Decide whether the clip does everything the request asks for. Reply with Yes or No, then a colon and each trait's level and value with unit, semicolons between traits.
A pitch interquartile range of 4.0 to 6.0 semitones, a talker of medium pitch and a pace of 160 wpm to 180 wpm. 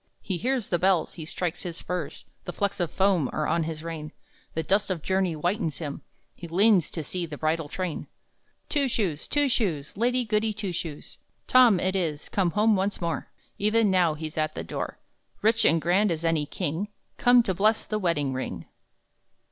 No: average, 4.5 semitones; medium, 180 Hz; average, 190 wpm